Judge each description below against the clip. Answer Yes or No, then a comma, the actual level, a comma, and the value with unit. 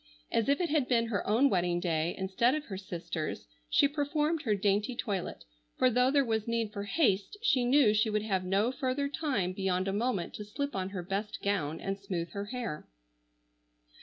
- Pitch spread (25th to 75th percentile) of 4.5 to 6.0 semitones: Yes, average, 5.1 semitones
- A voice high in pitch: Yes, high, 210 Hz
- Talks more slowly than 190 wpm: No, average, 195 wpm